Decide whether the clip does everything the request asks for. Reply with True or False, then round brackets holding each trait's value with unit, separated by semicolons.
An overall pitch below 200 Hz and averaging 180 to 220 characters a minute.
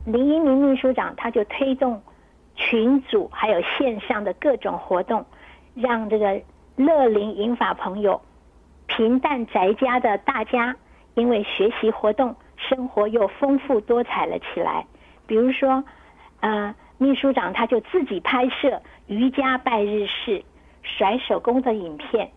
False (240 Hz; 205 characters per minute)